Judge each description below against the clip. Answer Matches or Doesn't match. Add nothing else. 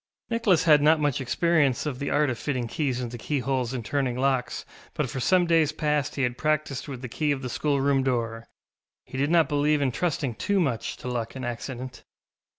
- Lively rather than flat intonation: Doesn't match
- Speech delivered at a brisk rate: Matches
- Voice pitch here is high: Doesn't match